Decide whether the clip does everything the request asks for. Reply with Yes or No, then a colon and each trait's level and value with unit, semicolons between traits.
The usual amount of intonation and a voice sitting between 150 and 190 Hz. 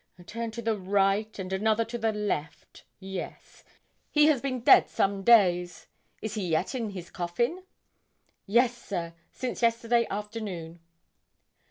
No: average, 3.9 semitones; high, 210 Hz